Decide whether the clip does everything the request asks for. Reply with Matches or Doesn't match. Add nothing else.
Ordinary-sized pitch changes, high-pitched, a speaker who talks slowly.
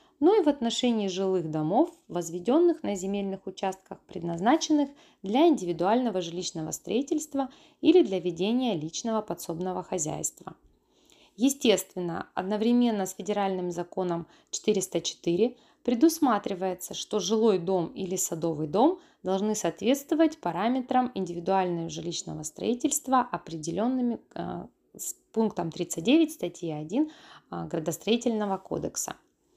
Doesn't match